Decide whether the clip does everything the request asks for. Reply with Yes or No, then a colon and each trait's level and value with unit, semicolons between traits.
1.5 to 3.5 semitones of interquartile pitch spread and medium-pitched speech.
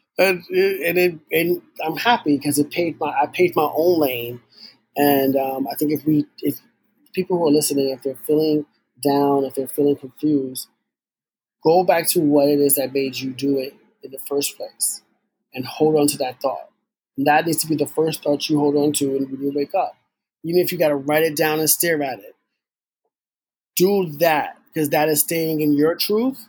Yes: average, 2.9 semitones; medium, 150 Hz